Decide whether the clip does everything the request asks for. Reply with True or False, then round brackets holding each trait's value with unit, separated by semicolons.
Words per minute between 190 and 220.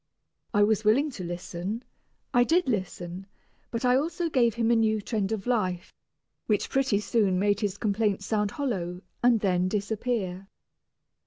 False (155 wpm)